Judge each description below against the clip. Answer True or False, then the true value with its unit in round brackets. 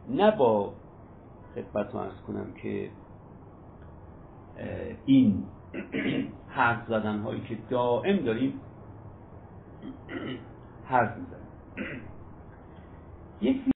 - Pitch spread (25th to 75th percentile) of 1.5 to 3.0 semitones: False (4.0 semitones)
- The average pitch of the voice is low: True (110 Hz)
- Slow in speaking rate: True (75 wpm)